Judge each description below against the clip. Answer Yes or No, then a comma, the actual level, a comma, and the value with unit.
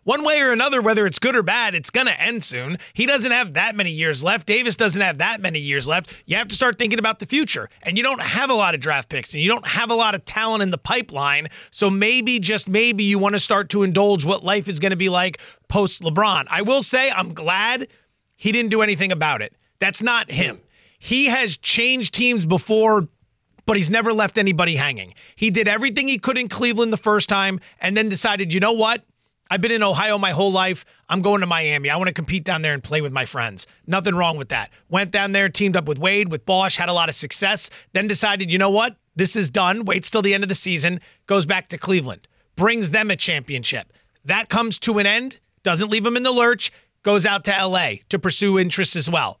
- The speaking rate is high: Yes, fast, 240 wpm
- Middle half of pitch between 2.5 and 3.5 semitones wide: No, average, 3.9 semitones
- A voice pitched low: No, high, 200 Hz